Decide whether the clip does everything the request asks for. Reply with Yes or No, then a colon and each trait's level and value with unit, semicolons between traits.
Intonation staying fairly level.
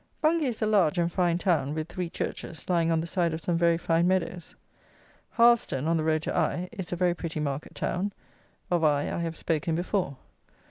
Yes: narrow, 2.2 semitones